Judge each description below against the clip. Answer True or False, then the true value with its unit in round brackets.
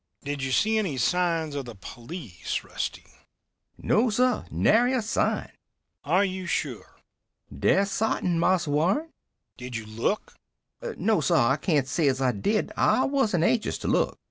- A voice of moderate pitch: True (170 Hz)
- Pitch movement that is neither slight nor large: False (8.1 semitones)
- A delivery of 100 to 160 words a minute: True (155 wpm)